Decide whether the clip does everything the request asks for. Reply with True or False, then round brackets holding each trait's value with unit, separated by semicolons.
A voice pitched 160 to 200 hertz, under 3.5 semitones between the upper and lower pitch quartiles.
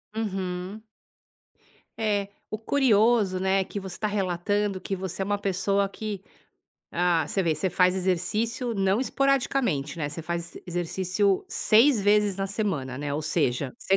True (195 Hz; 2.9 semitones)